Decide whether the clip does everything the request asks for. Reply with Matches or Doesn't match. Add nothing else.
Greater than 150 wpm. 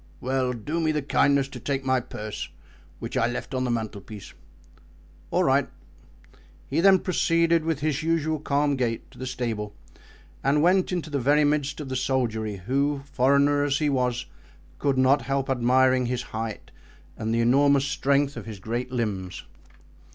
Matches